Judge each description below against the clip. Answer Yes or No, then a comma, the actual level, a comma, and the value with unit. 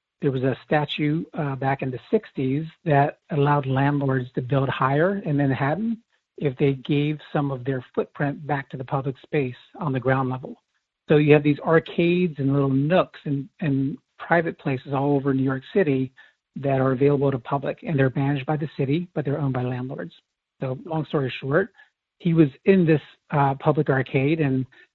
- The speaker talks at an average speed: Yes, average, 190 wpm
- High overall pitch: No, medium, 140 Hz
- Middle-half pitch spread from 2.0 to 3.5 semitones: Yes, narrow, 2.4 semitones